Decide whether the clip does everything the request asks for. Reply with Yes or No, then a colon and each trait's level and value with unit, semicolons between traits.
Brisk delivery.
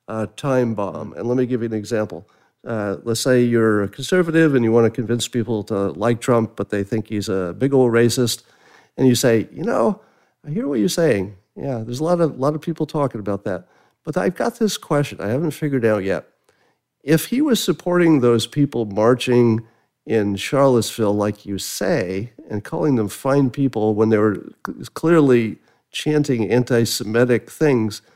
No: average, 190 wpm